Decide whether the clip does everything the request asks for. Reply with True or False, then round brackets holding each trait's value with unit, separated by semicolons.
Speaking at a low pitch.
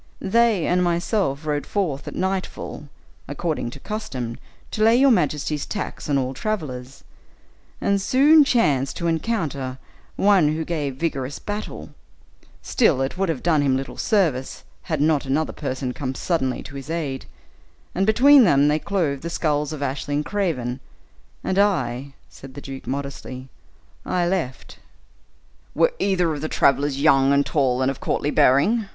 False (150 Hz)